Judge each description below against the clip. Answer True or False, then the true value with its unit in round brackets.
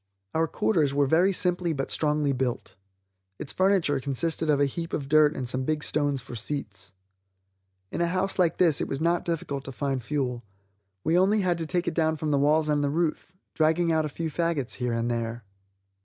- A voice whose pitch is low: False (150 Hz)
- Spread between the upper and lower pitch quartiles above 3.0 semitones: True (3.6 semitones)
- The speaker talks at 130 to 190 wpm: False (205 wpm)